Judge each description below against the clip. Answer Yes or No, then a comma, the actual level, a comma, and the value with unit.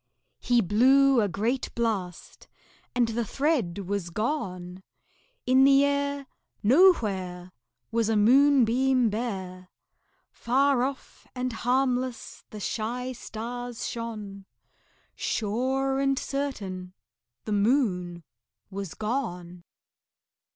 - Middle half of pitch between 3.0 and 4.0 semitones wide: No, average, 5.0 semitones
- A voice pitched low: No, high, 235 Hz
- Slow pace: Yes, slow, 95 wpm